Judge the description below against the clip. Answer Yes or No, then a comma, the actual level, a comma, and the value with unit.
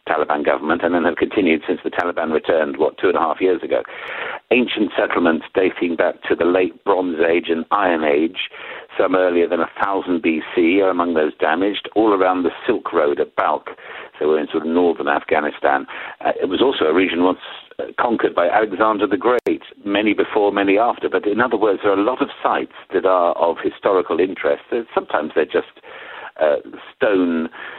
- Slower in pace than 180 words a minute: No, average, 190 wpm